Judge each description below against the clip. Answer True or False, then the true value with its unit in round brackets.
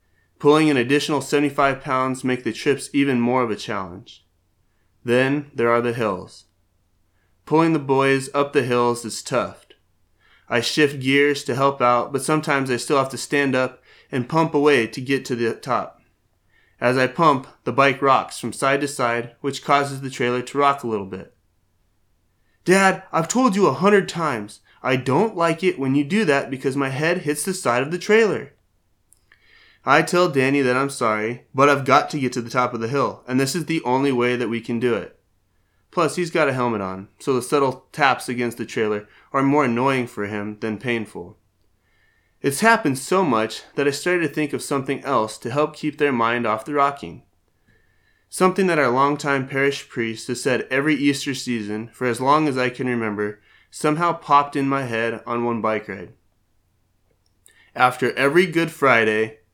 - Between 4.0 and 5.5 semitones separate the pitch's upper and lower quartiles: True (4.3 semitones)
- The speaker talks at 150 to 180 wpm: False (190 wpm)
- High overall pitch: False (130 Hz)